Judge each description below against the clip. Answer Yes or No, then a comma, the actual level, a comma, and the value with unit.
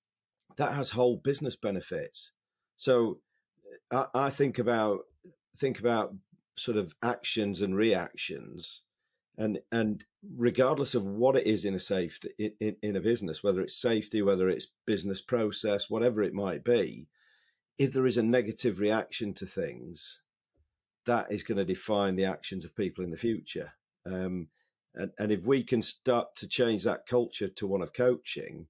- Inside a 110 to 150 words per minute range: No, average, 165 wpm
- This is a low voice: Yes, low, 110 Hz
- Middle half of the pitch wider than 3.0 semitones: Yes, average, 3.8 semitones